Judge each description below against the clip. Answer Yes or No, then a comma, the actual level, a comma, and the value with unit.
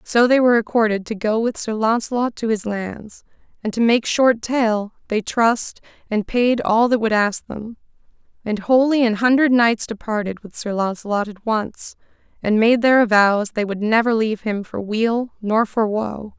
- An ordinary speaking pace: Yes, average, 185 wpm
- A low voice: No, high, 220 Hz